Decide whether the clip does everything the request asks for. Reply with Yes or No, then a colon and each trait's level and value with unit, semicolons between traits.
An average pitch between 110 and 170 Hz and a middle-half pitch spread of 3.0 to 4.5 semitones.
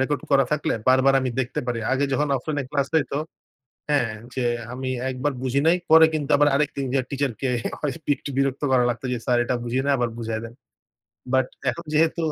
No: low, 135 Hz; narrow, 2.5 semitones